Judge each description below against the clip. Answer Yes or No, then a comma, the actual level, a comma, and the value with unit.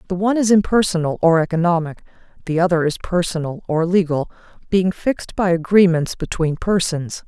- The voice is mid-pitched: Yes, medium, 175 Hz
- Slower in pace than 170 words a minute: Yes, average, 150 wpm